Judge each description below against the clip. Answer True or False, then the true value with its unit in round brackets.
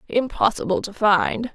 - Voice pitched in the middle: False (200 Hz)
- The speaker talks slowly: True (115 wpm)